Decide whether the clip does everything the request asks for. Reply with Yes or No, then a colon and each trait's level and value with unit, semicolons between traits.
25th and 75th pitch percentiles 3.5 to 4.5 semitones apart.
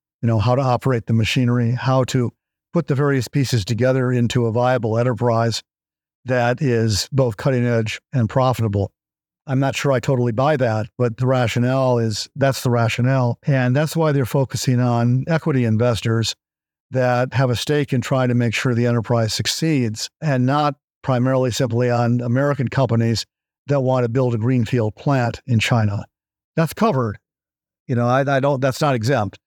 No: narrow, 2.4 semitones